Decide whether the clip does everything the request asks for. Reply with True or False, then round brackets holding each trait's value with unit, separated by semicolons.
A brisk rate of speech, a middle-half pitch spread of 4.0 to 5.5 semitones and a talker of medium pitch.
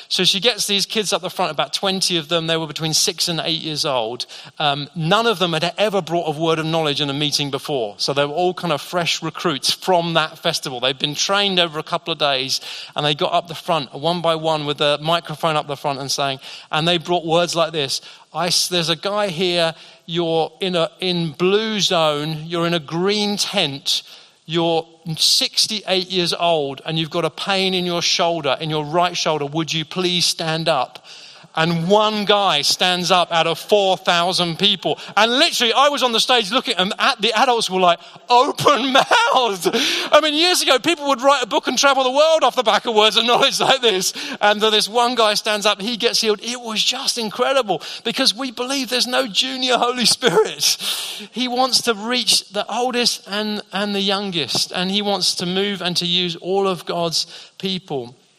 True (210 wpm; 4.8 semitones; 180 Hz)